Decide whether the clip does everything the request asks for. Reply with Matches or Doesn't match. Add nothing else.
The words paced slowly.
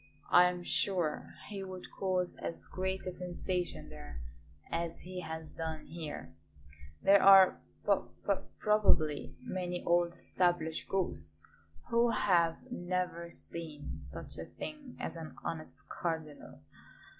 Matches